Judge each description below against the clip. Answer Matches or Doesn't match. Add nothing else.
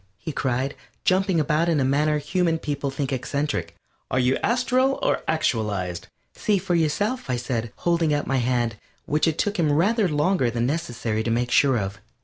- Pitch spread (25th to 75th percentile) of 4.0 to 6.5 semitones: Matches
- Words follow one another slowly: Doesn't match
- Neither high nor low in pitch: Matches